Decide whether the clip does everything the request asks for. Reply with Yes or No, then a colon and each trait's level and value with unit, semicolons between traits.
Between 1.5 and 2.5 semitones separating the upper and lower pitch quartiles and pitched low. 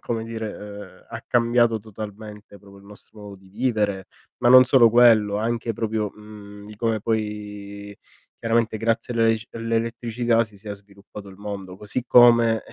Yes: narrow, 2.1 semitones; low, 110 Hz